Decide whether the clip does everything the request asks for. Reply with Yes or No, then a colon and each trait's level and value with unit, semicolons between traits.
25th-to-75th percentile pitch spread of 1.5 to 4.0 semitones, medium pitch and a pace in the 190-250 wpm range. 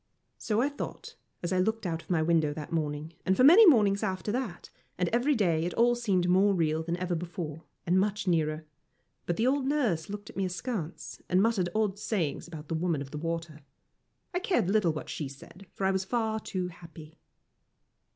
No: average, 4.7 semitones; medium, 180 Hz; fast, 205 wpm